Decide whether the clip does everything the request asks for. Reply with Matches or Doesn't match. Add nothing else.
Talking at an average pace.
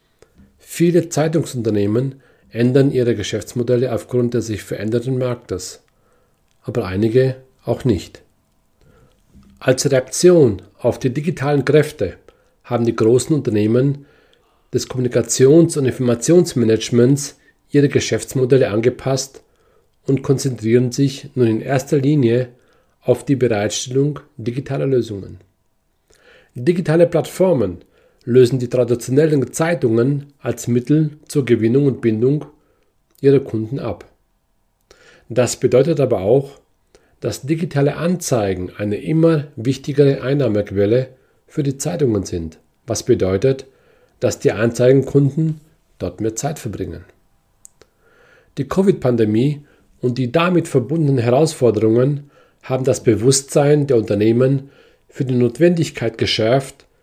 Doesn't match